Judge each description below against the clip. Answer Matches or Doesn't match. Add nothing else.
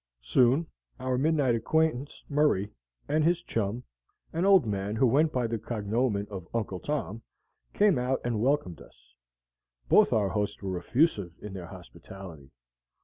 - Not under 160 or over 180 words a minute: Doesn't match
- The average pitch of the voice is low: Matches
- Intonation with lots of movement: Matches